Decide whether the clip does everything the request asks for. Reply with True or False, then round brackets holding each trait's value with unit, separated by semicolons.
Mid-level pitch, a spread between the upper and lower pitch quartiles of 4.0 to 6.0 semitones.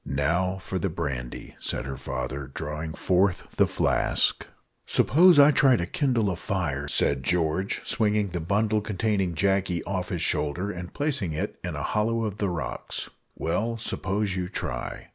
False (95 Hz; 4.7 semitones)